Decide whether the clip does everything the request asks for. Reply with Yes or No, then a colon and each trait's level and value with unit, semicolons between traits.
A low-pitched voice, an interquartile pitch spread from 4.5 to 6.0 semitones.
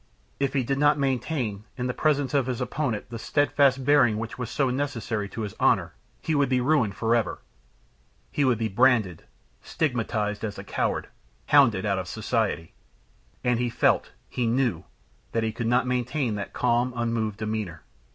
No: low, 120 Hz; average, 3.6 semitones